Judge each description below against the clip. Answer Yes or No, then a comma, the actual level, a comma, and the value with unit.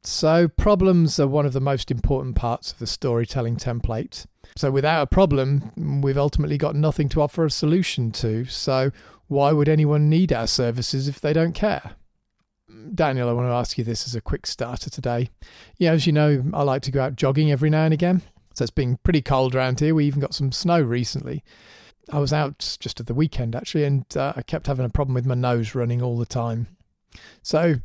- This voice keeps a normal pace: No, fast, 215 wpm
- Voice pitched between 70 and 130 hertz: No, medium, 140 Hz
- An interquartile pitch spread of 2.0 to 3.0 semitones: No, average, 3.8 semitones